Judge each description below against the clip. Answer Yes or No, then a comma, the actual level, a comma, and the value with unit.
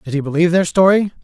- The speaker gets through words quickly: Yes, fast, 240 wpm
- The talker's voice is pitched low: No, medium, 170 Hz